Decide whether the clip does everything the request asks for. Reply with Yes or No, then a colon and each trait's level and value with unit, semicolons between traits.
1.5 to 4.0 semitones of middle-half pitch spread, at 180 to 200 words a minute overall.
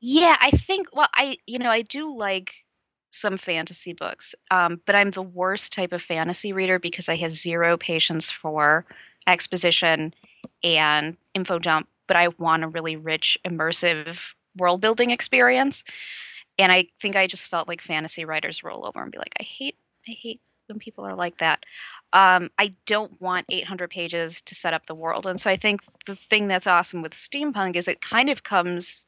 Yes: average, 3.7 semitones; average, 185 wpm